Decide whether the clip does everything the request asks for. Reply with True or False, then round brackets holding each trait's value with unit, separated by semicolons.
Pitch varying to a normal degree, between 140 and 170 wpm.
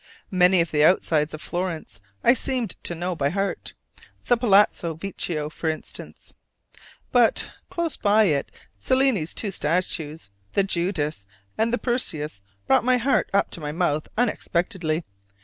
False (5.8 semitones; 145 wpm)